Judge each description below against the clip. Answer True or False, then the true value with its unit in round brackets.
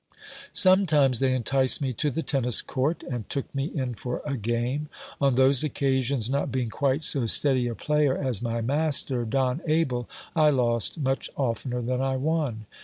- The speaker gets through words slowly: False (180 wpm)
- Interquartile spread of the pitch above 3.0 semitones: False (2.7 semitones)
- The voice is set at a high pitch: False (130 Hz)